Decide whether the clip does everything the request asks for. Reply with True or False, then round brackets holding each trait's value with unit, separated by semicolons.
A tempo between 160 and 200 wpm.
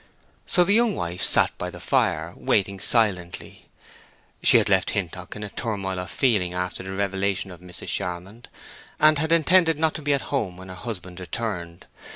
True (185 wpm)